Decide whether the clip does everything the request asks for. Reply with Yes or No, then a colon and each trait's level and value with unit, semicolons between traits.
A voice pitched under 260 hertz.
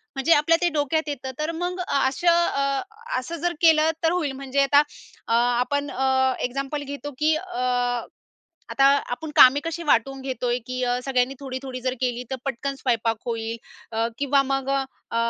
No: very high, 275 Hz